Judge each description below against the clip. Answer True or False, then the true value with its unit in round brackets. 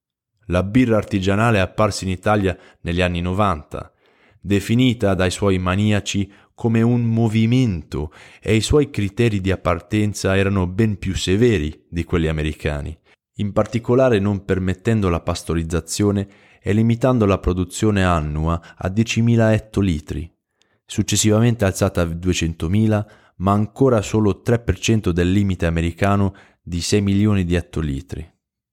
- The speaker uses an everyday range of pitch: True (3.5 semitones)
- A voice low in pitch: True (100 Hz)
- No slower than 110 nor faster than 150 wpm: True (125 wpm)